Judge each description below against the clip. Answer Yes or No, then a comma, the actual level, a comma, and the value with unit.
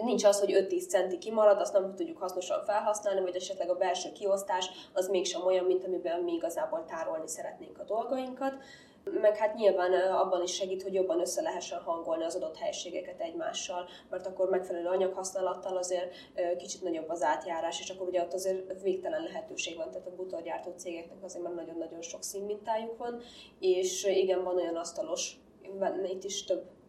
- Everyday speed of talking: No, fast, 170 wpm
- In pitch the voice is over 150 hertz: Yes, high, 190 Hz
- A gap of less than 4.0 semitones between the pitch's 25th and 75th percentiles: Yes, average, 2.9 semitones